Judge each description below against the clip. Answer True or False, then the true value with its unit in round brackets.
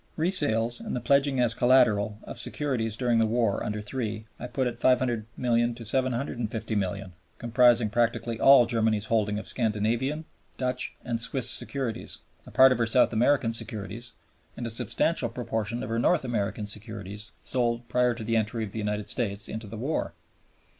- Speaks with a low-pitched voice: True (115 Hz)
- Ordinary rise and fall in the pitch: False (2.3 semitones)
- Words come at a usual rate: True (165 wpm)